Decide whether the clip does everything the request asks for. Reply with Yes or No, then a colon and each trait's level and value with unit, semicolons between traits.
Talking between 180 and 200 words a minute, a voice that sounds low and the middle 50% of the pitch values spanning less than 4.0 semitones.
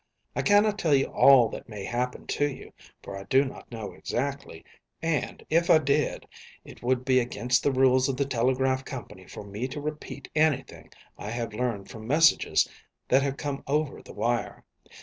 Yes: average, 185 wpm; low, 130 Hz; average, 3.2 semitones